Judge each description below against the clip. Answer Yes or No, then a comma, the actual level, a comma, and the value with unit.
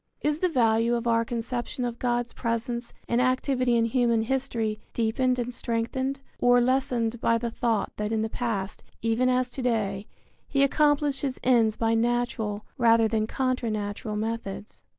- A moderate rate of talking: Yes, average, 165 wpm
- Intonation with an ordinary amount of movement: No, narrow, 2.1 semitones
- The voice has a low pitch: No, high, 235 Hz